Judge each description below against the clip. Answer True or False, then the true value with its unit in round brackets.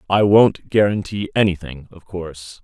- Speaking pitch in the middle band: False (95 Hz)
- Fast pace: False (135 wpm)